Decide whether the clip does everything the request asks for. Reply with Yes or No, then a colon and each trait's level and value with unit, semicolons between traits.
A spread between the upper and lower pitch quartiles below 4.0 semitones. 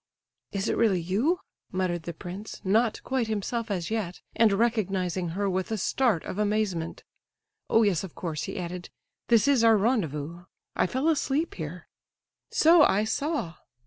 No: average, 4.5 semitones